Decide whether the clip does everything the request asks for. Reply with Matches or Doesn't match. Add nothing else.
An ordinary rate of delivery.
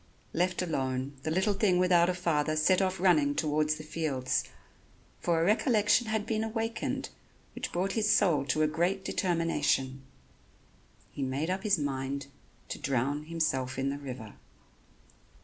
Matches